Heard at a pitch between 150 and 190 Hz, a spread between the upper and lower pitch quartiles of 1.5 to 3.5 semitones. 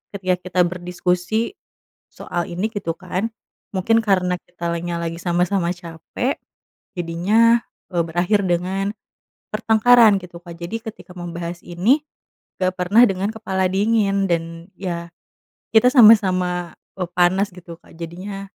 Yes: medium, 185 Hz; average, 2.8 semitones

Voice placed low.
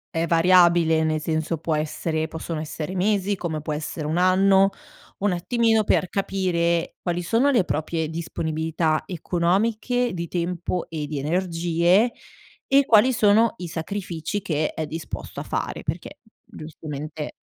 No: medium, 170 Hz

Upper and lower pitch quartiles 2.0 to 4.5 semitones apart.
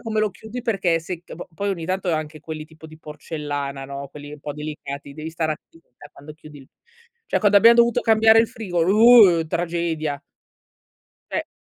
No: average, 5.1 semitones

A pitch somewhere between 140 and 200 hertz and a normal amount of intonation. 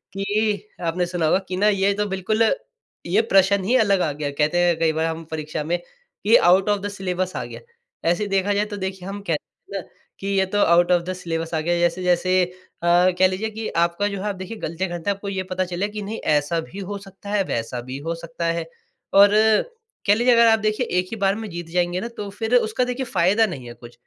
Yes: medium, 185 Hz; average, 3.2 semitones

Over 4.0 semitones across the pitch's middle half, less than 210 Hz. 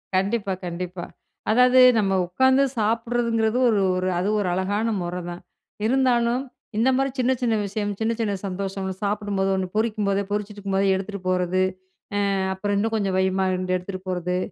No: average, 3.2 semitones; high, 200 Hz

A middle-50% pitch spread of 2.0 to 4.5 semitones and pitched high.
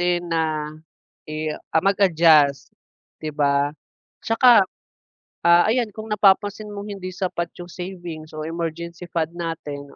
No: average, 3.5 semitones; medium, 170 Hz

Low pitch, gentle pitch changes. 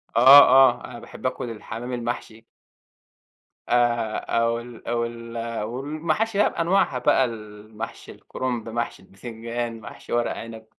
Yes: low, 120 Hz; narrow, 1.7 semitones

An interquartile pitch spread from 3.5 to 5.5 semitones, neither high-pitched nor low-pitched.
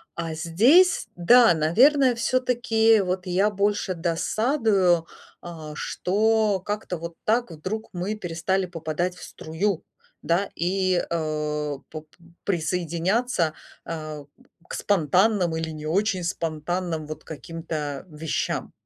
Yes: average, 4.5 semitones; medium, 180 Hz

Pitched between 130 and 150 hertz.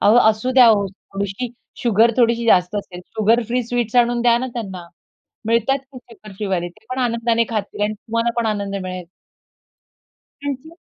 No: high, 230 Hz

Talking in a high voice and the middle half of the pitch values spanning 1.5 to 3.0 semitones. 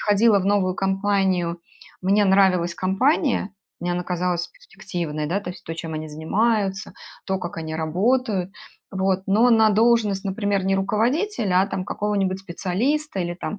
Yes: high, 195 Hz; average, 2.7 semitones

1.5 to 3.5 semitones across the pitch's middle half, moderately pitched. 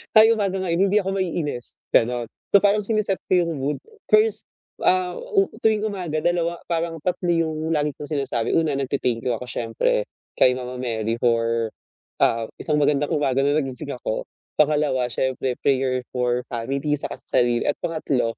No: wide, 5.8 semitones; medium, 145 Hz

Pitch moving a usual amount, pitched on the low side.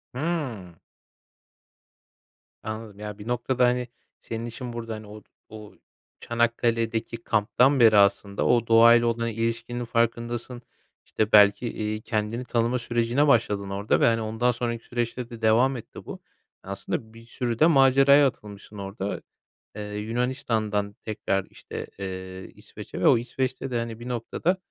No: narrow, 2.3 semitones; low, 115 Hz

